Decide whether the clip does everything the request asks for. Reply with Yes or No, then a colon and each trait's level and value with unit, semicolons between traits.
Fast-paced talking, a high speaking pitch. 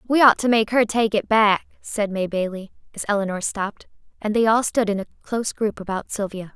Yes: fast, 220 wpm; high, 210 Hz